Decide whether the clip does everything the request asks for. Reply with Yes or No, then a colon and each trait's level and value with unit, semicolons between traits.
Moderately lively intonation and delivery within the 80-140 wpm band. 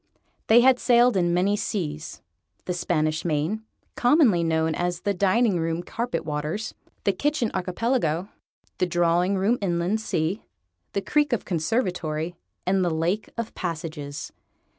Yes: average, 5.0 semitones; slow, 135 wpm